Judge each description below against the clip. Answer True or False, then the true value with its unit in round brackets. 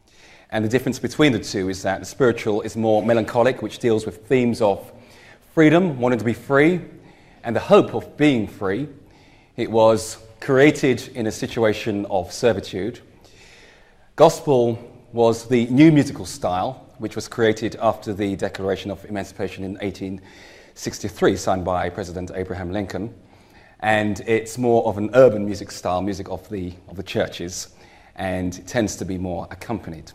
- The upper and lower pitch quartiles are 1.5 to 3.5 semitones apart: False (4.1 semitones)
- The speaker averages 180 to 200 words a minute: False (155 wpm)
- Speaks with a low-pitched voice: True (110 Hz)